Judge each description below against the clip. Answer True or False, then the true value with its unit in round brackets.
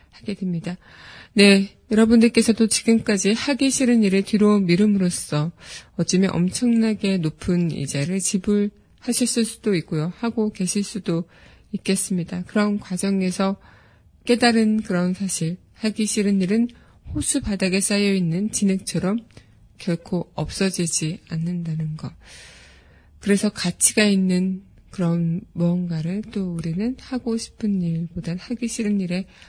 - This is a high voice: True (195 Hz)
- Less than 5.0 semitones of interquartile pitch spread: True (3.7 semitones)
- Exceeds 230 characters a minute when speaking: True (280 characters per minute)